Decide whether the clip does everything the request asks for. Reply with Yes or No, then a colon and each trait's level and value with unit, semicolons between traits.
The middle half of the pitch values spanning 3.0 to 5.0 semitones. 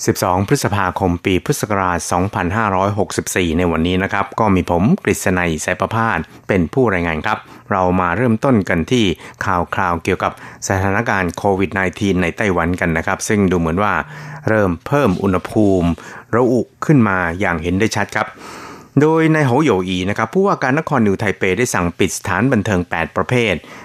Yes: average, 3.7 semitones